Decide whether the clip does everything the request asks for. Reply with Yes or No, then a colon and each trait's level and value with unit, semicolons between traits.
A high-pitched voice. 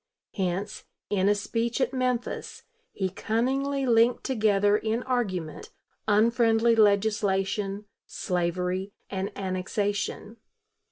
Yes: high, 210 Hz